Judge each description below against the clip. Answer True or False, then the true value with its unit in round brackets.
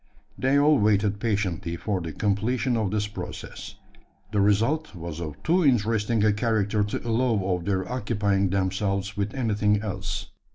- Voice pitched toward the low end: True (105 Hz)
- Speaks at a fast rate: False (155 wpm)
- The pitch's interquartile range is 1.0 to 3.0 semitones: True (2.5 semitones)